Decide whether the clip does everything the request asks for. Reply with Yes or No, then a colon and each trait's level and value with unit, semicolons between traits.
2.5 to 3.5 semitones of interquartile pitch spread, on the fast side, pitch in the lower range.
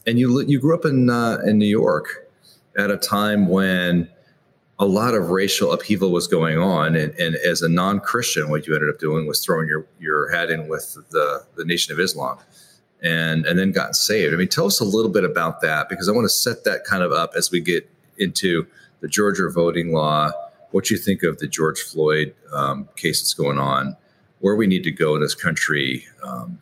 No: average, 5.2 semitones; fast, 215 wpm; very low, 85 Hz